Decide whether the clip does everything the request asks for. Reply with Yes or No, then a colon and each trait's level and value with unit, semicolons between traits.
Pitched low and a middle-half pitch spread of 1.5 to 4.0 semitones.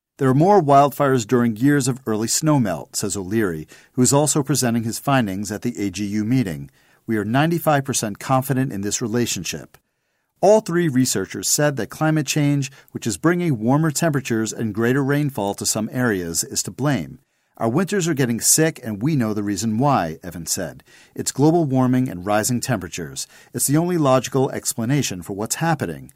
No: low, 125 Hz; average, 5.0 semitones